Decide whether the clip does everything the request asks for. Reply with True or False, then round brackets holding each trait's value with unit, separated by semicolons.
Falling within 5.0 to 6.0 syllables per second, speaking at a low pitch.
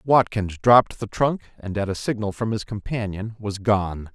False (4.7 syllables/s; 105 Hz)